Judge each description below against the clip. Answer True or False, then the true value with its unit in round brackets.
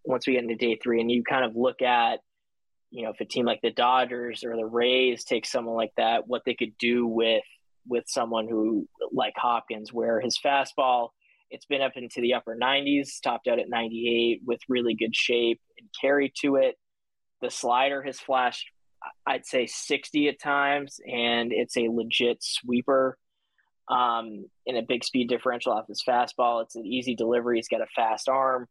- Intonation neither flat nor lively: False (2.3 semitones)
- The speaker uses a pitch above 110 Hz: True (120 Hz)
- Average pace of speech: True (190 wpm)